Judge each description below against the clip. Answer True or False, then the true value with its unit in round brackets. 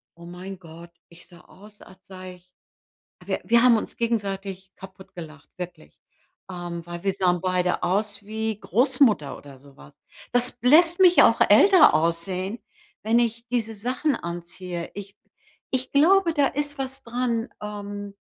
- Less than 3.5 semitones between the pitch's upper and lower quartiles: False (5.3 semitones)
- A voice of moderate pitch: False (200 Hz)